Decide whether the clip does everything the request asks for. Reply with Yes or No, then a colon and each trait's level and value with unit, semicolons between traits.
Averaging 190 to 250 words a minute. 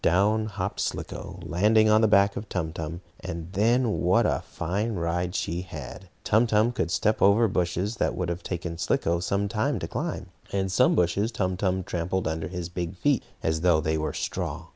Yes: average, 195 wpm